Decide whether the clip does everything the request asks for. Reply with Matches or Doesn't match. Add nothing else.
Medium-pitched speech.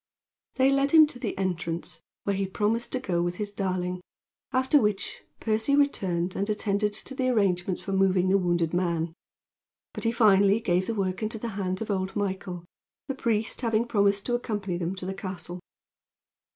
Doesn't match